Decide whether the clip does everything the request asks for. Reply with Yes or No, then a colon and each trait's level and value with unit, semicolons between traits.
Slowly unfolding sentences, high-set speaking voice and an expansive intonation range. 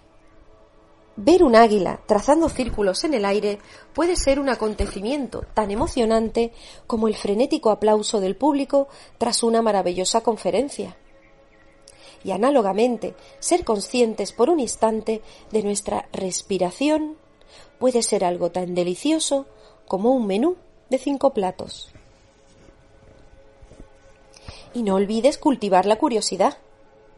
Yes: slow, 115 wpm; high, 215 Hz; wide, 6.1 semitones